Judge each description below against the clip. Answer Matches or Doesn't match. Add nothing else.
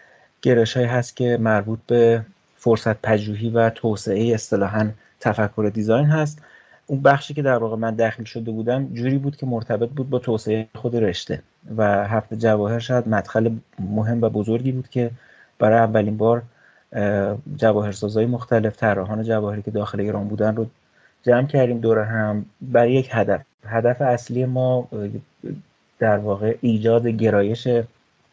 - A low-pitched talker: Matches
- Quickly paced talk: Doesn't match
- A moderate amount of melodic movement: Doesn't match